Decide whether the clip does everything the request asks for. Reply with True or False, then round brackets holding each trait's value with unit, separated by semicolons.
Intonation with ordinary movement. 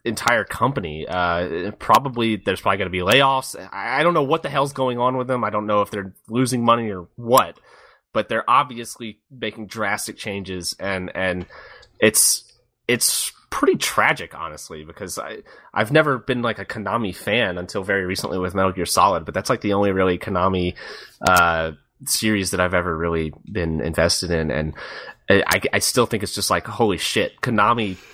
True (4.7 semitones)